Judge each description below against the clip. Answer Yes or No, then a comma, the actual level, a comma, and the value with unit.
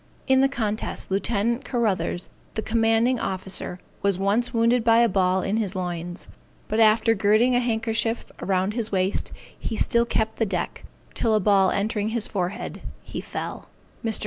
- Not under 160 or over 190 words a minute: Yes, average, 165 wpm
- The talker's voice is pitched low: No, high, 220 Hz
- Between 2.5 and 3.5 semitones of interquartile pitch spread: Yes, average, 3.1 semitones